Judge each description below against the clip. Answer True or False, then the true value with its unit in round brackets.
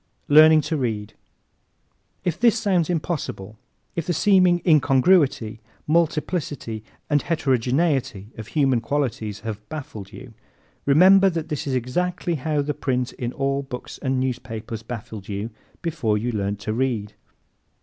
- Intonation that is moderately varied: False (6.1 semitones)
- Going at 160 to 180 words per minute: False (140 wpm)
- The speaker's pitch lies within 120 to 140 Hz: True (135 Hz)